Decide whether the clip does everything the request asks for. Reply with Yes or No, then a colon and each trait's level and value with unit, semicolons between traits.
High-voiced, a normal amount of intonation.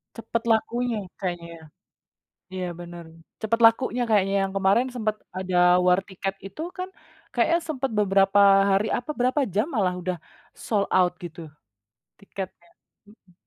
Yes: high, 200 Hz; average, 3.8 semitones